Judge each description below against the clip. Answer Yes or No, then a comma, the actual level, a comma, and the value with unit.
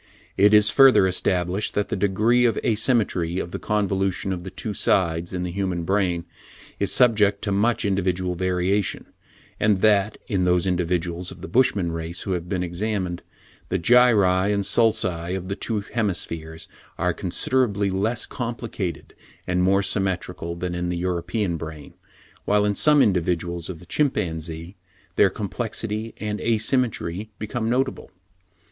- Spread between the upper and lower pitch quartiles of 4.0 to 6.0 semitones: No, average, 3.2 semitones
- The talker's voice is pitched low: Yes, very low, 95 Hz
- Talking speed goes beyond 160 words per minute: No, average, 150 wpm